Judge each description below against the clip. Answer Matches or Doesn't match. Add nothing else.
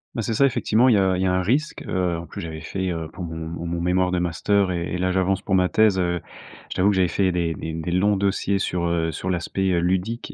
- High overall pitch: Doesn't match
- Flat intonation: Matches